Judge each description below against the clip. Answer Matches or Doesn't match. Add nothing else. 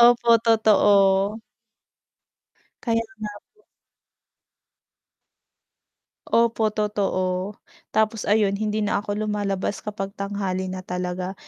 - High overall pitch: Matches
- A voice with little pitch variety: Matches